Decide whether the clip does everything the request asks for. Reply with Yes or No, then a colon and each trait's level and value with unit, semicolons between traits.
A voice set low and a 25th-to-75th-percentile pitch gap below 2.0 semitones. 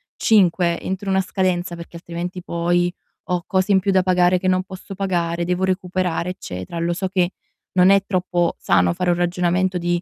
No: medium, 180 Hz; narrow, 1.4 semitones